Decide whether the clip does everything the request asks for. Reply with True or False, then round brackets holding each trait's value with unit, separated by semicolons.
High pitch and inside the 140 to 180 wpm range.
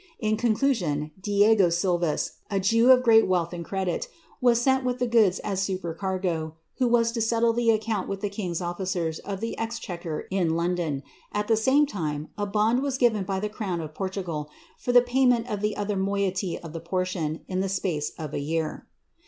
False (195 Hz; 200 wpm)